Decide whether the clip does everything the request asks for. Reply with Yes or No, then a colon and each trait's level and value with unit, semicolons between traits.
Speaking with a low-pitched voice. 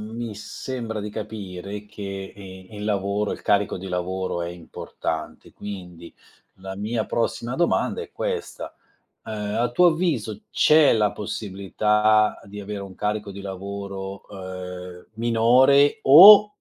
Yes: low, 105 Hz